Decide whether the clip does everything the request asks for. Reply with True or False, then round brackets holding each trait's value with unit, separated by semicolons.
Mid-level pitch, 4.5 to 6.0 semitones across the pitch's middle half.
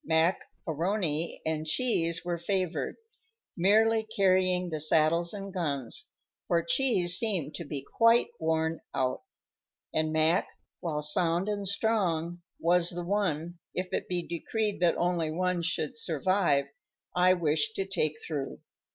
False (175 Hz; 3.2 semitones)